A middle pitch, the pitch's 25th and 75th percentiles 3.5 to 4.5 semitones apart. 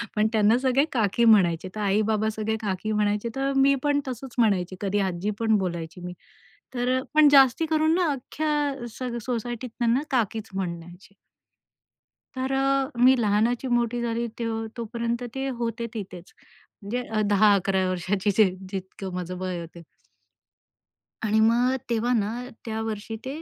No: high, 225 Hz; average, 4.0 semitones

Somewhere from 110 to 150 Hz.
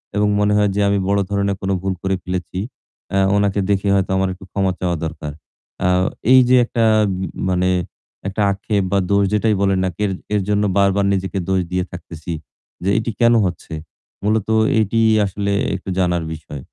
No: low, 100 Hz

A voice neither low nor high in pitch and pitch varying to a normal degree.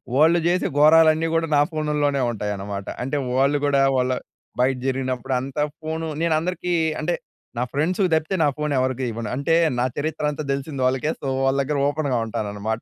Yes: medium, 145 Hz; average, 3.5 semitones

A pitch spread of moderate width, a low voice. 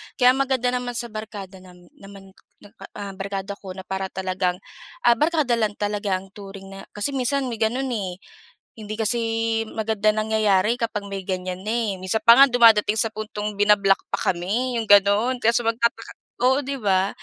No: average, 3.2 semitones; high, 210 Hz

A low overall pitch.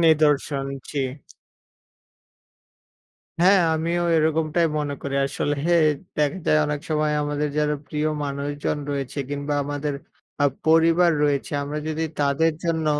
No: medium, 150 Hz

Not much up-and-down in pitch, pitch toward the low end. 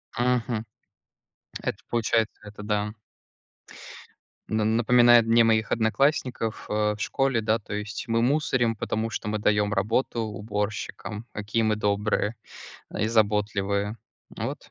Yes: narrow, 1.8 semitones; low, 110 Hz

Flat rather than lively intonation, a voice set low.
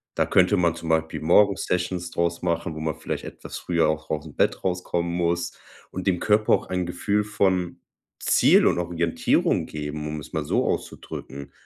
Yes: narrow, 2.2 semitones; very low, 85 Hz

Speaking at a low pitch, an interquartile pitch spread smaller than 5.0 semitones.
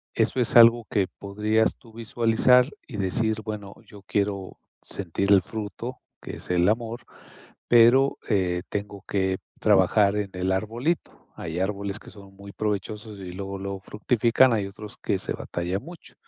Yes: low, 105 Hz; average, 2.7 semitones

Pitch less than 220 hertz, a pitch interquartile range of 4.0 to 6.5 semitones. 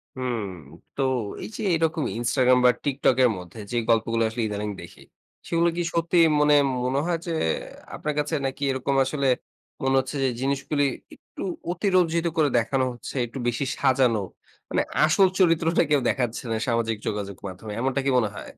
Yes: low, 135 Hz; average, 4.7 semitones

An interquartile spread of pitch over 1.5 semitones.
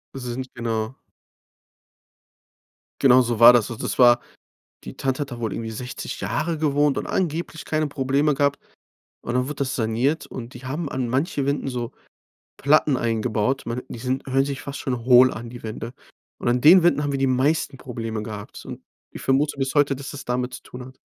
Yes: average, 2.9 semitones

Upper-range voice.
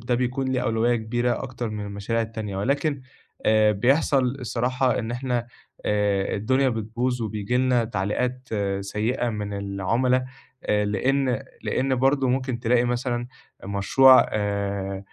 No: low, 120 Hz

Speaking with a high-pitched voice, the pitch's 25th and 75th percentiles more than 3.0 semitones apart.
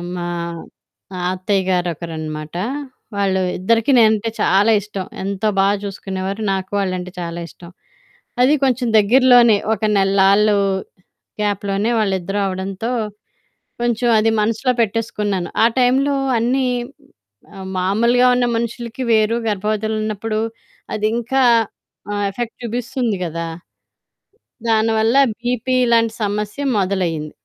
Yes: high, 210 Hz; average, 3.4 semitones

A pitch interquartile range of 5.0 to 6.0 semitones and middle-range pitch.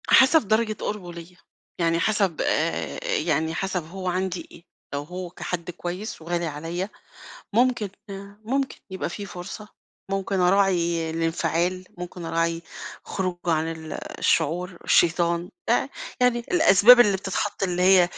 No: average, 2.9 semitones; medium, 180 Hz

